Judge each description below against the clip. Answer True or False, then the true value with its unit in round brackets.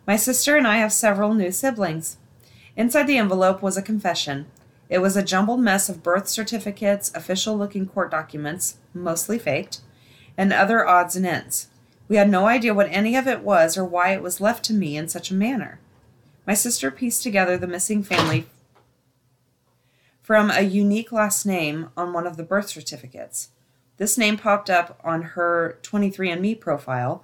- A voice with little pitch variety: False (5.2 semitones)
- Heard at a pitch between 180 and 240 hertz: True (185 Hz)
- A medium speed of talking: True (175 wpm)